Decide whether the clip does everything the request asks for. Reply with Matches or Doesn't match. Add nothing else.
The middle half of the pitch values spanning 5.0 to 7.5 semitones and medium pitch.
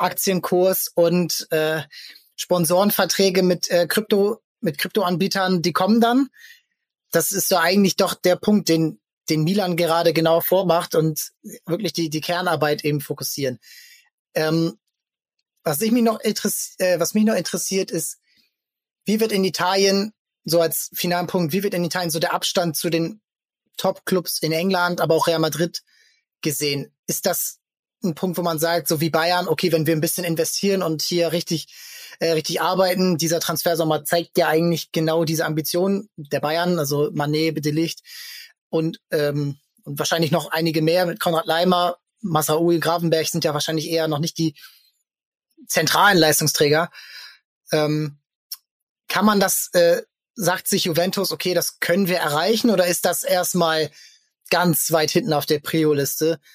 Doesn't match